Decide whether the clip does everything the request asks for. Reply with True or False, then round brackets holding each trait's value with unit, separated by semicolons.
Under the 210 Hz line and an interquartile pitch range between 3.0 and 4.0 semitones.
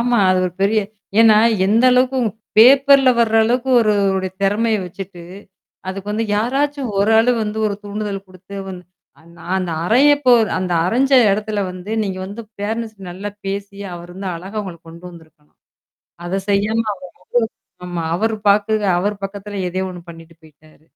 True (200 Hz; 3.4 semitones)